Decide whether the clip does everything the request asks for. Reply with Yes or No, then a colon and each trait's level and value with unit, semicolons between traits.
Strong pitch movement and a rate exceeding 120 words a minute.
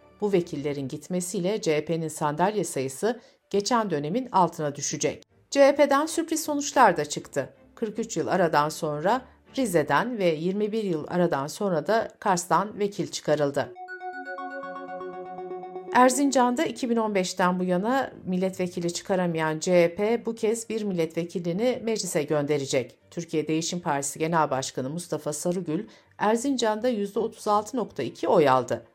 No: wide, 6.1 semitones; average, 110 wpm